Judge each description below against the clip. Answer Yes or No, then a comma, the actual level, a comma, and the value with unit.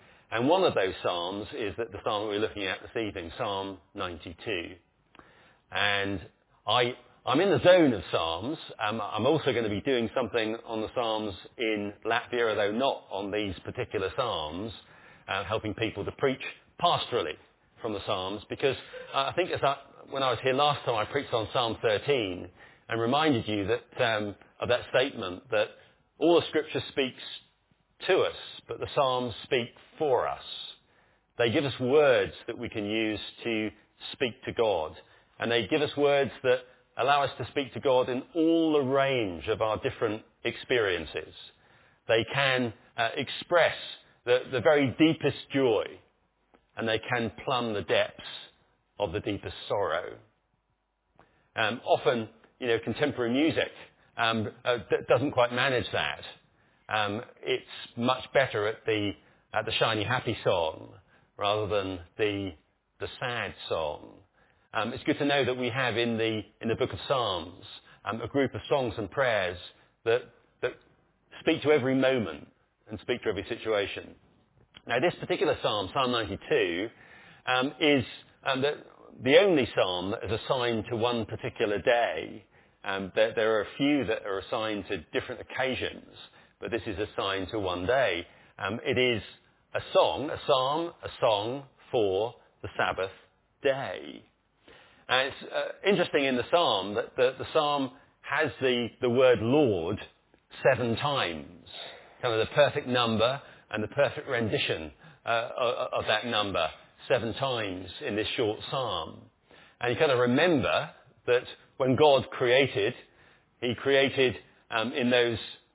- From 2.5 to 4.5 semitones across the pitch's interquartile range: No, average, 5.1 semitones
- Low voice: Yes, low, 120 Hz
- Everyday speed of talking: Yes, average, 160 wpm